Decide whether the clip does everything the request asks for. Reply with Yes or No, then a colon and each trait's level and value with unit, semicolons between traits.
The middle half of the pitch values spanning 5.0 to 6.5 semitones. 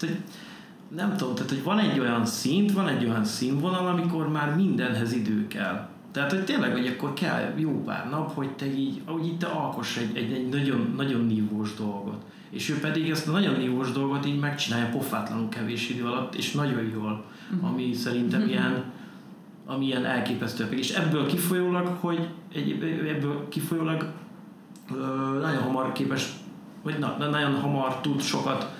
Yes: average, 5.3 semitones